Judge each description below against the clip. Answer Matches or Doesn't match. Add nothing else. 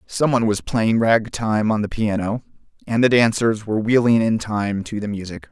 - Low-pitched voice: Matches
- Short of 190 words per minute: Doesn't match